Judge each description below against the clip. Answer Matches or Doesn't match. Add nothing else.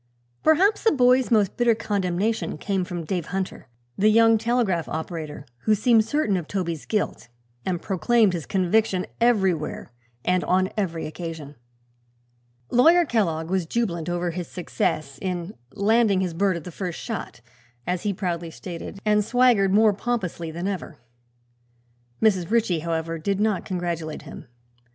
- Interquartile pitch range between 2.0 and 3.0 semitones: Doesn't match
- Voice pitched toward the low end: Doesn't match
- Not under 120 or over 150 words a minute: Matches